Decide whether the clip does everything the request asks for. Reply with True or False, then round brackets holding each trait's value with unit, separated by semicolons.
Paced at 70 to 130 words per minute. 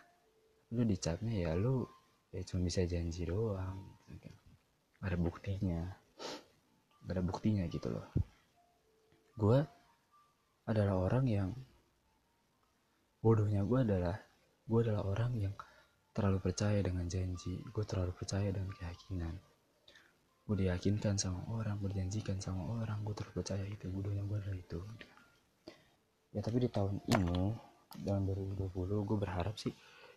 True (120 wpm)